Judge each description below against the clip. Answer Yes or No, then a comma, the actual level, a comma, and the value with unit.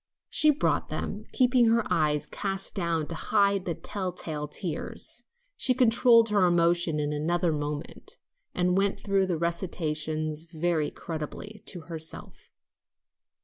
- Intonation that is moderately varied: Yes, average, 4.2 semitones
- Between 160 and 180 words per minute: No, slow, 135 wpm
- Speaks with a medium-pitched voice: Yes, medium, 175 Hz